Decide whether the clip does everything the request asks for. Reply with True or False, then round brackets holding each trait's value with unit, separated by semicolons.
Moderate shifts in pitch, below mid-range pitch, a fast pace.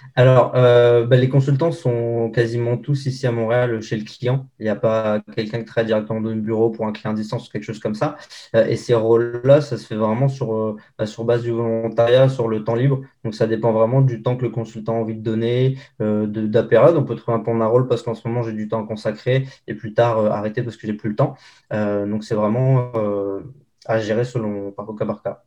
False (2.1 semitones; 115 Hz; 255 wpm)